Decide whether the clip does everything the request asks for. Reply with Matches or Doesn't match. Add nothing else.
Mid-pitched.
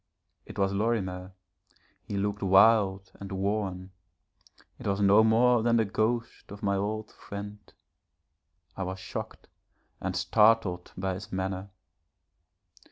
Doesn't match